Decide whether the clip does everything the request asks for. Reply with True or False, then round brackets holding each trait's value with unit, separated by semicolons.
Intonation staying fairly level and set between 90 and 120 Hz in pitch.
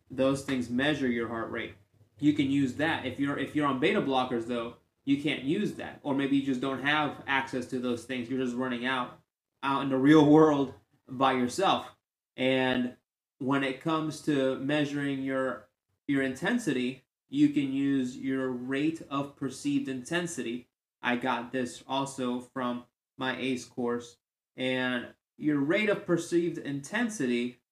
False (2.3 semitones; 135 Hz)